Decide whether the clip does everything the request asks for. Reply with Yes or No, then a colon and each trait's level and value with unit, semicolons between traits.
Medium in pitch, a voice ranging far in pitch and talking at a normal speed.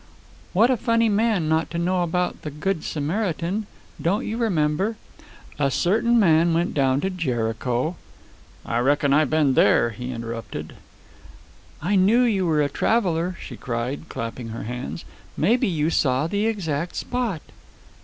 Yes: medium, 165 Hz; wide, 6.3 semitones; average, 155 wpm